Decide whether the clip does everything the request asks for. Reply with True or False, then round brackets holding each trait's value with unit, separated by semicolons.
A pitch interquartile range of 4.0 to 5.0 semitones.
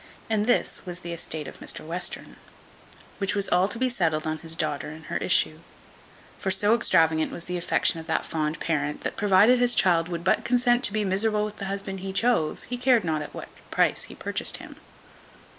True (4.6 semitones)